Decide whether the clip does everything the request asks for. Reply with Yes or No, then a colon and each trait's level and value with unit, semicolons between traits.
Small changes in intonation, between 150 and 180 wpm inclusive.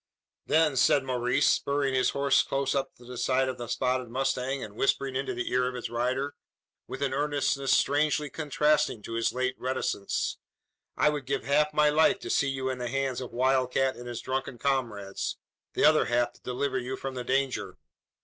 No: narrow, 1.8 semitones; average, 195 wpm